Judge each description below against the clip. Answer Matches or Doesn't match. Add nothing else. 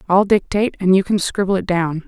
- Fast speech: Matches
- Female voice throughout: Matches